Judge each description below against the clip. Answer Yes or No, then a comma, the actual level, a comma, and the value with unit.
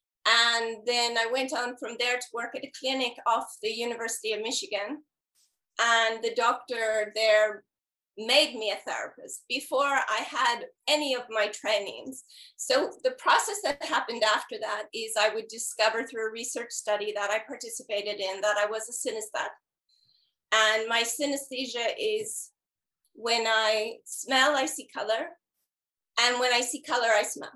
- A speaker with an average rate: Yes, average, 160 wpm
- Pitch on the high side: Yes, high, 235 Hz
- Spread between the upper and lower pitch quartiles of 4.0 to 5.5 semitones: No, average, 3.5 semitones